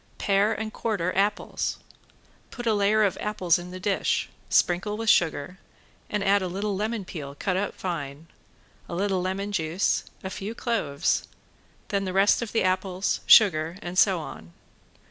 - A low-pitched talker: No, high, 195 Hz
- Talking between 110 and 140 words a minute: No, average, 165 wpm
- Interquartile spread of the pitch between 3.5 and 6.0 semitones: No, average, 2.8 semitones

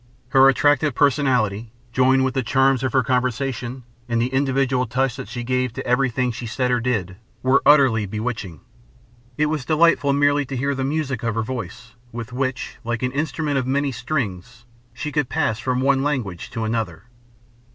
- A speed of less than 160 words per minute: No, average, 180 wpm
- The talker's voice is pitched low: Yes, low, 130 Hz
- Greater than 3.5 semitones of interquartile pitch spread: No, narrow, 2.6 semitones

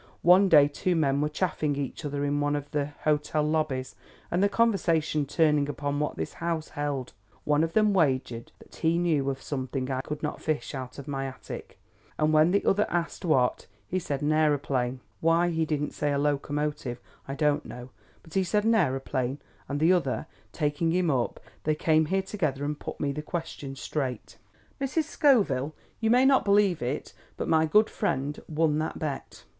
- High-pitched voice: No, medium, 150 Hz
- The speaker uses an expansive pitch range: No, average, 3.2 semitones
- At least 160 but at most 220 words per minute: Yes, average, 190 wpm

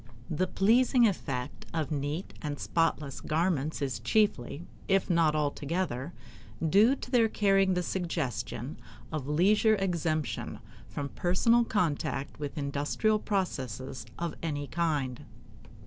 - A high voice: No, medium, 165 Hz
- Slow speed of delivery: Yes, slow, 115 wpm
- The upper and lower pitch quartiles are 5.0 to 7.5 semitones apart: Yes, average, 5.3 semitones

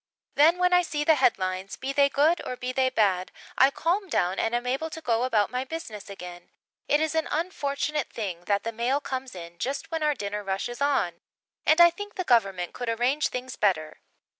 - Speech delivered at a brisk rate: Yes, fast, 215 wpm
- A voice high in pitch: Yes, very high, 255 Hz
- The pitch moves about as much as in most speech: No, wide, 6.9 semitones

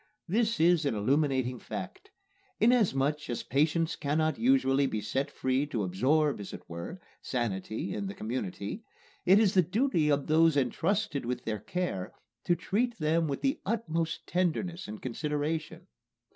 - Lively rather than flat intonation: Yes, wide, 5.9 semitones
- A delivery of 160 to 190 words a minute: No, average, 150 wpm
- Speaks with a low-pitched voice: No, medium, 155 Hz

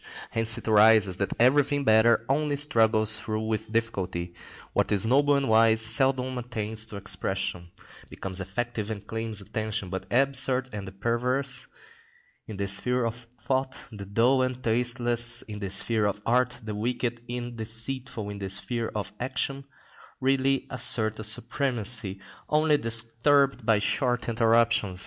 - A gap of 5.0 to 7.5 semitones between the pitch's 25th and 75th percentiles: No, average, 3.1 semitones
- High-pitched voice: No, low, 115 Hz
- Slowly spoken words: No, average, 150 wpm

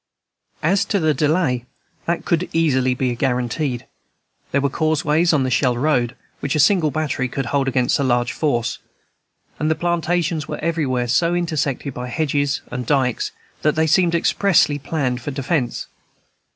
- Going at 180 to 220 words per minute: No, average, 160 wpm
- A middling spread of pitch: Yes, average, 4.0 semitones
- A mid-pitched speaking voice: Yes, medium, 145 Hz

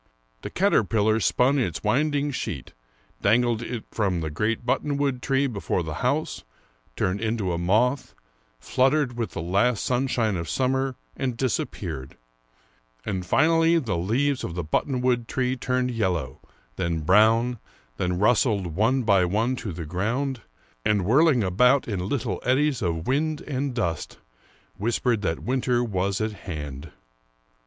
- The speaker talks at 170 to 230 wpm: No, average, 145 wpm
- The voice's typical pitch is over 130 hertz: No, low, 115 Hz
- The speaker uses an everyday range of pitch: No, wide, 5.7 semitones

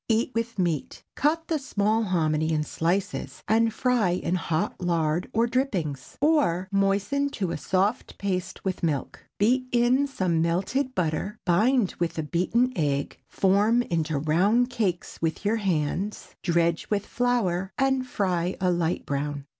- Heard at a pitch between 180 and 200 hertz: Yes, high, 190 Hz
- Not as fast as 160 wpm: Yes, average, 150 wpm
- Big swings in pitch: Yes, wide, 5.8 semitones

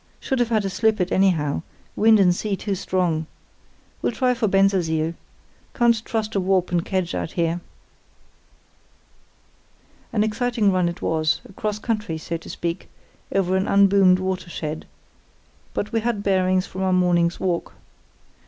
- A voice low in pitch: No, high, 190 Hz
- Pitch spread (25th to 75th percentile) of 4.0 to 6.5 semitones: No, average, 3.3 semitones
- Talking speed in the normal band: Yes, average, 155 wpm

